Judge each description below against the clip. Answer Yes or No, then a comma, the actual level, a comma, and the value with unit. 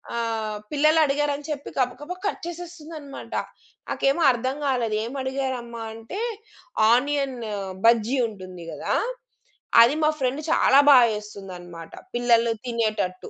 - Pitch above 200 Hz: Yes, very high, 250 Hz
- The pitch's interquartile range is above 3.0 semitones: Yes, average, 4.2 semitones